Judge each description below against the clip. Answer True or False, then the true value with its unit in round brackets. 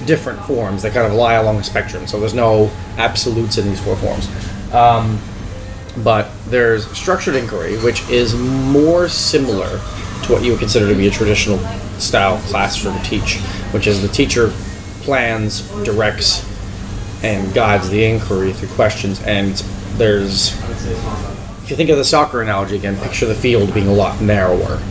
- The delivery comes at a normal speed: True (160 wpm)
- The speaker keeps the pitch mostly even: True (2.3 semitones)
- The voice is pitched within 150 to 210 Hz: False (105 Hz)